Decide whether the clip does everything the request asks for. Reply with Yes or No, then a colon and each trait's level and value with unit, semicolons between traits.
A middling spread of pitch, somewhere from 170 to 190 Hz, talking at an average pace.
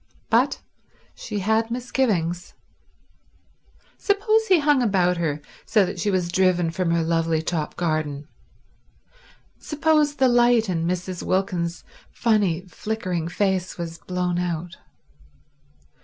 No: average, 4.9 semitones; medium, 185 Hz; slow, 110 wpm